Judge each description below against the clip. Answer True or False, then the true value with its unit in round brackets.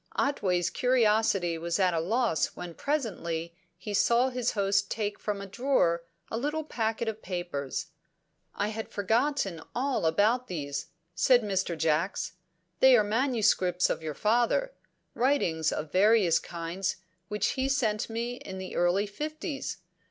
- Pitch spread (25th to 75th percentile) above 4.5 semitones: True (5.6 semitones)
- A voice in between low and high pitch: False (205 Hz)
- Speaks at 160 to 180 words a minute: False (145 wpm)